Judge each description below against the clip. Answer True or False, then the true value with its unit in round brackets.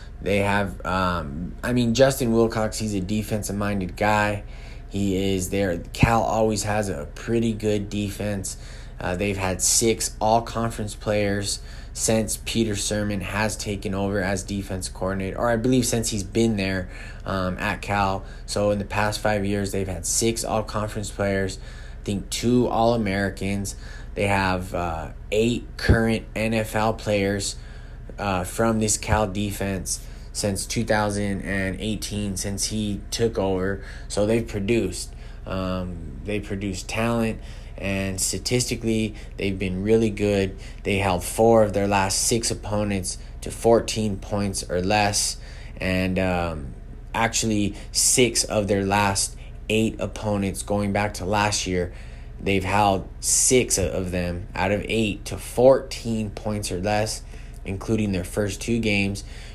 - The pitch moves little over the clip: True (2.3 semitones)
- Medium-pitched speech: False (100 Hz)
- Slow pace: False (145 wpm)